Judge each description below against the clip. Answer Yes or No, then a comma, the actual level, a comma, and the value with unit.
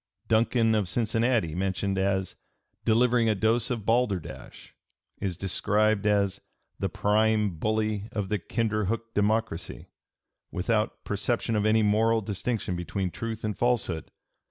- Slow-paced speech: Yes, slow, 130 wpm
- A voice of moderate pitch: No, low, 105 Hz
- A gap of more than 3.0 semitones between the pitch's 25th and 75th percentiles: No, narrow, 2.5 semitones